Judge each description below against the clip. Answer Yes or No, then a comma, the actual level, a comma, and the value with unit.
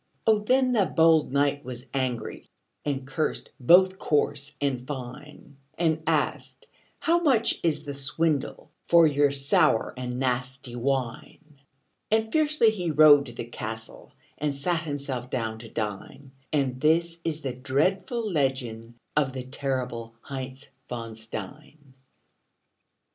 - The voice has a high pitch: No, medium, 140 Hz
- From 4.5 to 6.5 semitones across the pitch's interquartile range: No, average, 4.1 semitones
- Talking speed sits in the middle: No, slow, 130 wpm